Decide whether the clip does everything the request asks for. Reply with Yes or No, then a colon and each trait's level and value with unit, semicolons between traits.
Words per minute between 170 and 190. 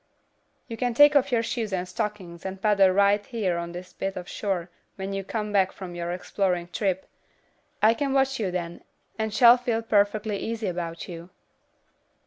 Yes: average, 180 wpm